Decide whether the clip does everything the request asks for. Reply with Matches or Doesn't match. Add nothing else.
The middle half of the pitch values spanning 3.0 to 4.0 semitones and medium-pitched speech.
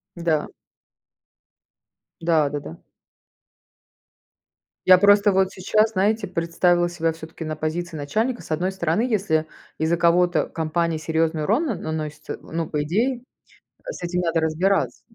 Matches